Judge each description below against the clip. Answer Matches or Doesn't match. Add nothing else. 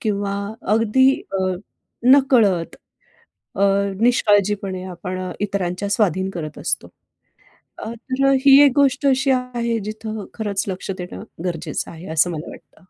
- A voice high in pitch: Matches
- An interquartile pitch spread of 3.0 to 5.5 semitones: Matches